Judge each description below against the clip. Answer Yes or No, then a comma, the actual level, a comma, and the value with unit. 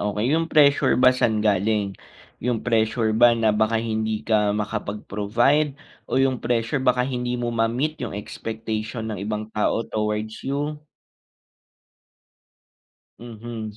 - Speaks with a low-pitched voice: Yes, low, 115 Hz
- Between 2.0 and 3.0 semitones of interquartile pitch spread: Yes, narrow, 2.6 semitones